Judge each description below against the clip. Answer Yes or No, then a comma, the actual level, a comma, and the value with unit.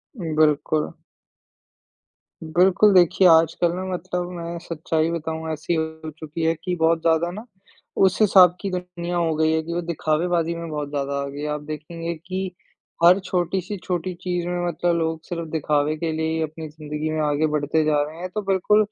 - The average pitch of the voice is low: No, medium, 165 Hz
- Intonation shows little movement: Yes, narrow, 2.2 semitones